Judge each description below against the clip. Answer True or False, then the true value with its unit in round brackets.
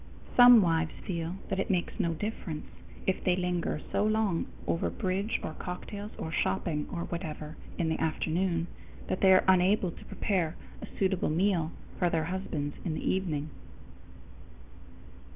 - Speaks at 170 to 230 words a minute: False (155 wpm)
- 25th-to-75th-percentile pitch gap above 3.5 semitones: False (2.9 semitones)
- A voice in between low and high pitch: True (180 Hz)